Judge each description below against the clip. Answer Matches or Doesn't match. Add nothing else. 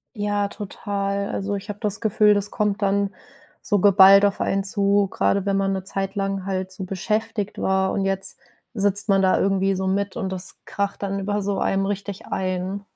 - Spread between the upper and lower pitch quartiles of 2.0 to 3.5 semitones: Doesn't match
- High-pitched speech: Matches